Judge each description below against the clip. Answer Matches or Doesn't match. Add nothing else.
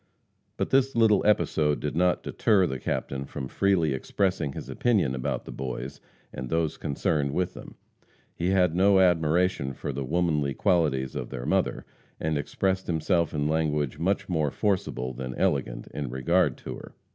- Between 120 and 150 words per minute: Doesn't match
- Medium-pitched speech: Doesn't match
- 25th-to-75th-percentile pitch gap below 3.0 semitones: Doesn't match